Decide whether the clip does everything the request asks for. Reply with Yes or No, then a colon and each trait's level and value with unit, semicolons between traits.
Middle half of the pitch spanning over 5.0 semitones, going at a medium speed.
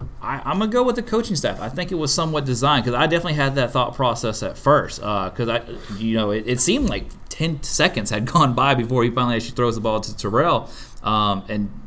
No: wide, 5.6 semitones; fast, 250 wpm